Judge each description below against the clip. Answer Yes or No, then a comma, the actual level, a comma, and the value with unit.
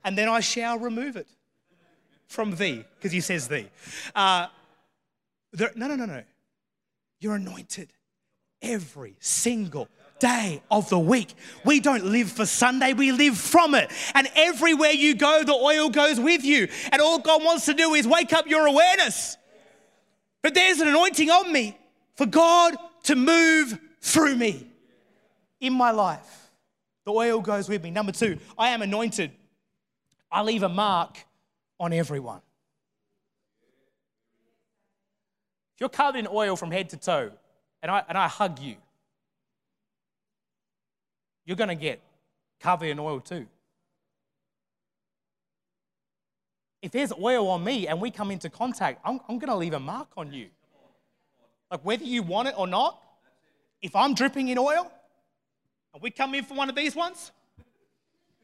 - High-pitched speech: Yes, high, 230 Hz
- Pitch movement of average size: No, wide, 6.8 semitones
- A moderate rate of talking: Yes, average, 150 wpm